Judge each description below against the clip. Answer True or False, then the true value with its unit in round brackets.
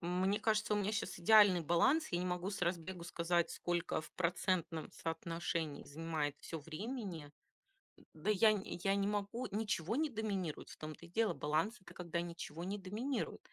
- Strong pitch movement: False (3.8 semitones)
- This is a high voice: False (180 Hz)